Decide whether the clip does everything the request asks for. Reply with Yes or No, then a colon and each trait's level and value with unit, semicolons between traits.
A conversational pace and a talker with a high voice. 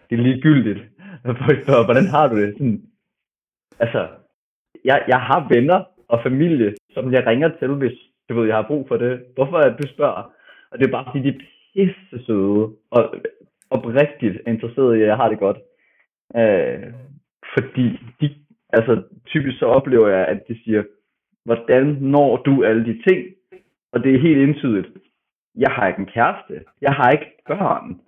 No: average, 170 wpm; low, 130 Hz